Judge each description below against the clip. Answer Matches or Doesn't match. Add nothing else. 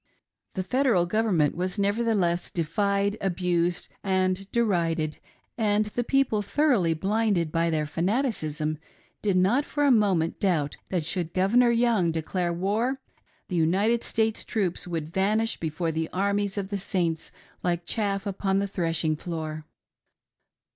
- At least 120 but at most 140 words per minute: Matches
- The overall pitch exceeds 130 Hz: Matches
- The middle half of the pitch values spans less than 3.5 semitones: Doesn't match